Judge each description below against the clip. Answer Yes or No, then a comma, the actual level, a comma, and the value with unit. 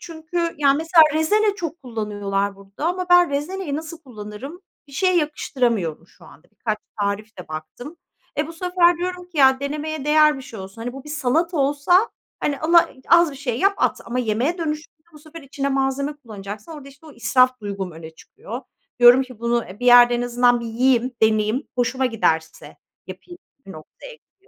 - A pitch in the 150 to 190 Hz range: No, very high, 270 Hz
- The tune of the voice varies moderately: No, wide, 5.8 semitones